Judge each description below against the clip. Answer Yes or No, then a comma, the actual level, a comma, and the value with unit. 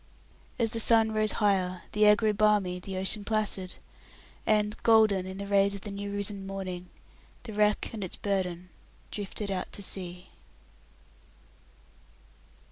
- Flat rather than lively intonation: Yes, narrow, 2.0 semitones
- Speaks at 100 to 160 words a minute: Yes, average, 145 wpm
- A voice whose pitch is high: Yes, high, 200 Hz